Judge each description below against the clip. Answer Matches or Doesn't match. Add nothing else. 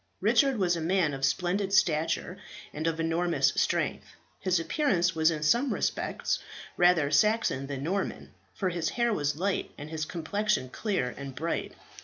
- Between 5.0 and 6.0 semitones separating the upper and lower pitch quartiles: Doesn't match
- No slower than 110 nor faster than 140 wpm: Doesn't match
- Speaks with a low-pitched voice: Doesn't match